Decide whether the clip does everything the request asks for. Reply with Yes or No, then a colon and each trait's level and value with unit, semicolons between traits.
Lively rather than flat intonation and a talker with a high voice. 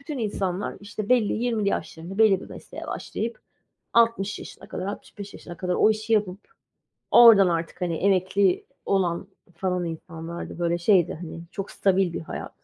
No: average, 3.5 semitones; high, 195 Hz